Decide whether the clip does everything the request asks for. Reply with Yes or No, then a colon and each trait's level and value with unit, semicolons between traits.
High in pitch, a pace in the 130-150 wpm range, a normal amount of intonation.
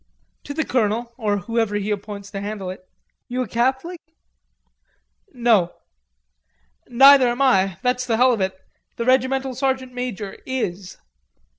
Yes: high, 235 Hz; average, 140 wpm; average, 4.2 semitones